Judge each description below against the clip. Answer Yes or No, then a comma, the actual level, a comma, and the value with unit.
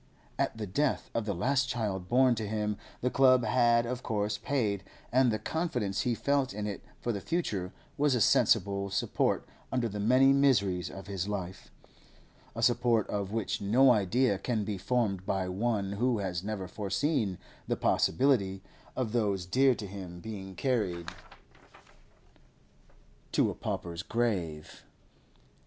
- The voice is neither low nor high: No, low, 105 Hz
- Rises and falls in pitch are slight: No, average, 4.3 semitones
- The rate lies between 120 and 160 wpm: Yes, average, 150 wpm